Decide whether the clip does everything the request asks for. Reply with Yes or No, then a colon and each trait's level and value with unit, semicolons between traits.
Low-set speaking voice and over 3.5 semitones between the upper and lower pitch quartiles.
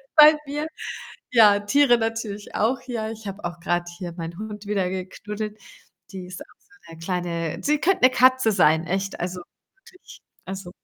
No: high, 205 Hz; average, 4.2 semitones